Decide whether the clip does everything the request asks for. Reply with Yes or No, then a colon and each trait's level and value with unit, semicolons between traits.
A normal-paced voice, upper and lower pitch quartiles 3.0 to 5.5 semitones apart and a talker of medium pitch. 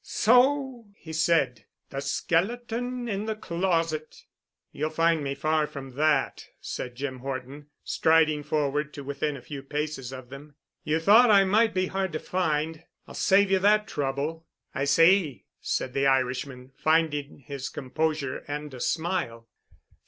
Yes: average, 150 wpm; average, 5.1 semitones; medium, 155 Hz